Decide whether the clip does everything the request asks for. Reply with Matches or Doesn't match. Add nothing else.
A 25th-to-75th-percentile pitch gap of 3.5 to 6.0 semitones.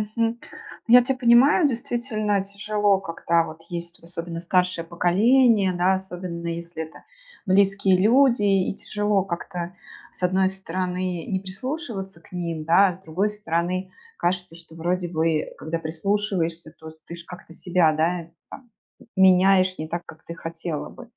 Doesn't match